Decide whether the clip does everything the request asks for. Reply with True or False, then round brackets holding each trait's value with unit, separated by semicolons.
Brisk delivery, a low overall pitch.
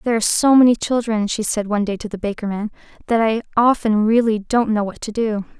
False (245 wpm; 220 Hz)